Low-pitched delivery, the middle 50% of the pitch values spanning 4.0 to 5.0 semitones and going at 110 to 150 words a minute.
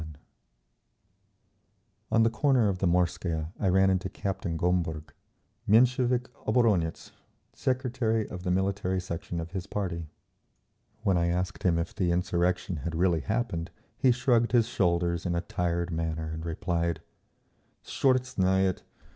Yes: very low, 90 Hz; average, 4.3 semitones; average, 140 wpm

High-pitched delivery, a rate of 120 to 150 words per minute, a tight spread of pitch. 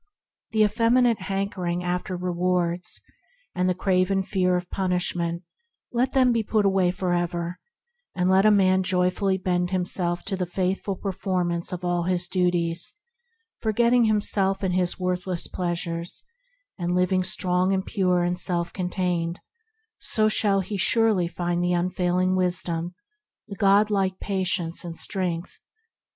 No: medium, 180 Hz; average, 140 wpm; narrow, 1.7 semitones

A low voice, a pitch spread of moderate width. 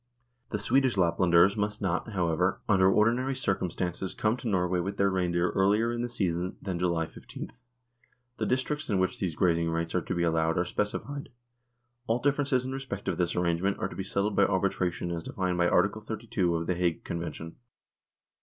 Yes: very low, 95 Hz; average, 3.7 semitones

